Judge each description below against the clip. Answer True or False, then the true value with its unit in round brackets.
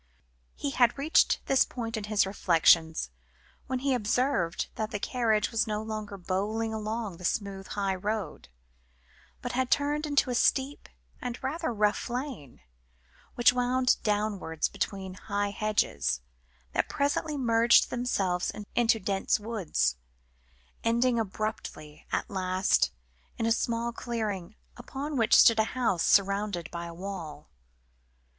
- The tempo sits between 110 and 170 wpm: True (135 wpm)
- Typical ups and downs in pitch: True (4.1 semitones)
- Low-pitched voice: False (215 Hz)